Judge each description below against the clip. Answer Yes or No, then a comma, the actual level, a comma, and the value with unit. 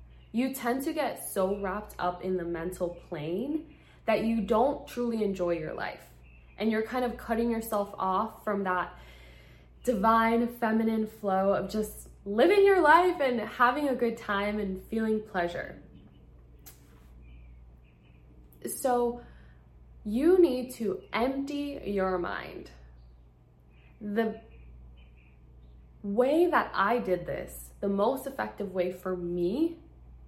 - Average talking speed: No, slow, 125 wpm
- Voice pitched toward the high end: Yes, high, 200 Hz